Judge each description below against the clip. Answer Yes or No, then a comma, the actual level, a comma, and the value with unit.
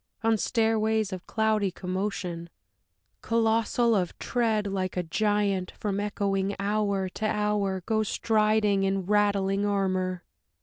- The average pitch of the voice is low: No, high, 205 Hz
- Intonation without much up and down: Yes, narrow, 2.1 semitones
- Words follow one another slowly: Yes, slow, 120 wpm